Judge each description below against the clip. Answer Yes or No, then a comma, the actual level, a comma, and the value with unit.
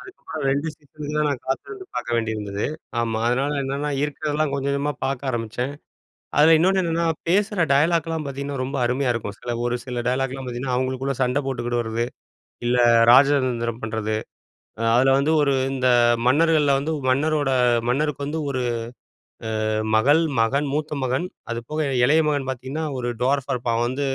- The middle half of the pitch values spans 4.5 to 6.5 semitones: No, average, 3.3 semitones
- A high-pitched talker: No, low, 135 Hz